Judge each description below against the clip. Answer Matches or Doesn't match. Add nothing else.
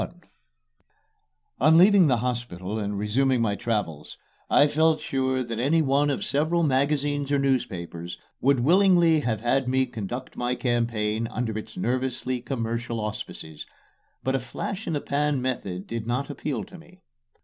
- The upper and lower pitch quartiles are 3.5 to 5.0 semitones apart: Matches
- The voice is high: Doesn't match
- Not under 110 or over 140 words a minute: Doesn't match